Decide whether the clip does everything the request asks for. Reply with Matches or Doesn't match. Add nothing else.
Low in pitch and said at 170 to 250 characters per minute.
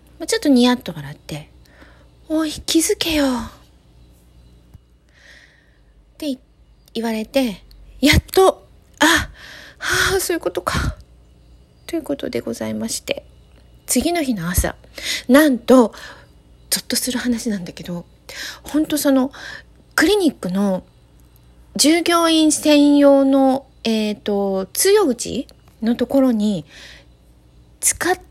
Doesn't match